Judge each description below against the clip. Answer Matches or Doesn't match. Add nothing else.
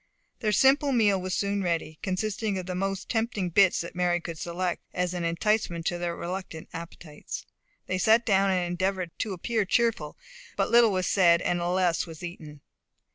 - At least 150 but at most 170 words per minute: Doesn't match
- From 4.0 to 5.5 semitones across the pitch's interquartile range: Doesn't match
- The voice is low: Doesn't match